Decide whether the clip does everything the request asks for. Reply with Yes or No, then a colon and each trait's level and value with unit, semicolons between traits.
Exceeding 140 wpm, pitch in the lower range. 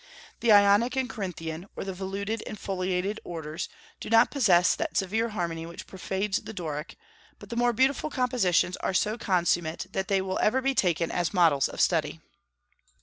No: average, 175 wpm; high, 190 Hz